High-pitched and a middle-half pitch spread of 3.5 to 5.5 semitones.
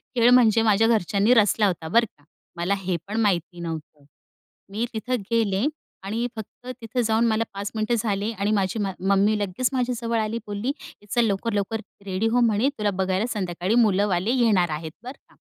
No: high, 210 Hz; average, 2.9 semitones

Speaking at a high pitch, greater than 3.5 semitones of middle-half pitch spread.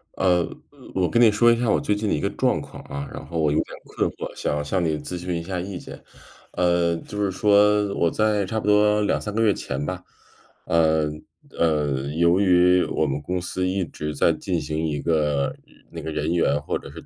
No: very low, 90 Hz; average, 4.5 semitones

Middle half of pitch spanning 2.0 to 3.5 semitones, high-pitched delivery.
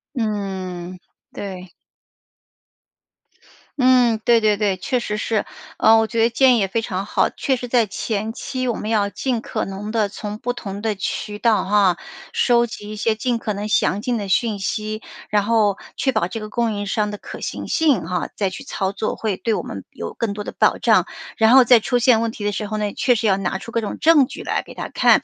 Yes: narrow, 2.6 semitones; high, 215 Hz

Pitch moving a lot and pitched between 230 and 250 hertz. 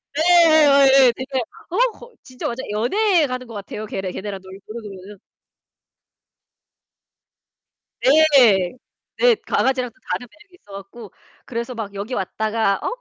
Yes: wide, 5.8 semitones; high, 245 Hz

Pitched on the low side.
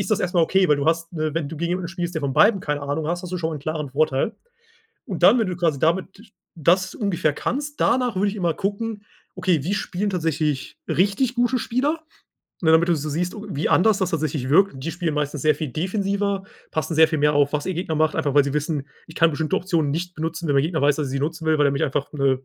No: medium, 165 Hz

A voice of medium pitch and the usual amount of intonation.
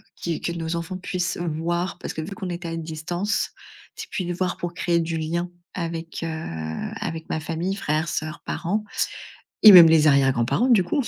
No: medium, 170 Hz; narrow, 2.0 semitones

